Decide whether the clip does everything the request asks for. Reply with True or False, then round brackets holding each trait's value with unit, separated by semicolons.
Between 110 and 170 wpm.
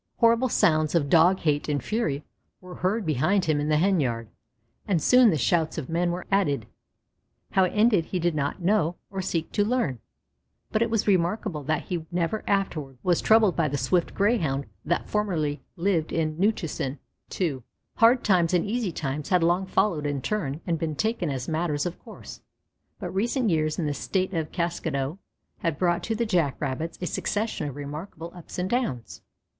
False (185 wpm)